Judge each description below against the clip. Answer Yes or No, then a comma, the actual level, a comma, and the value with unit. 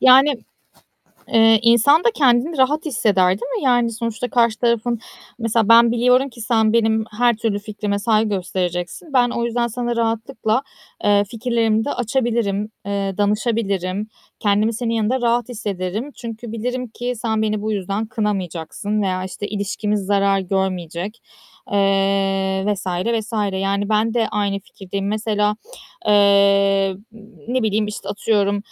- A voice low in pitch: No, high, 215 Hz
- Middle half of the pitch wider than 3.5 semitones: No, average, 2.8 semitones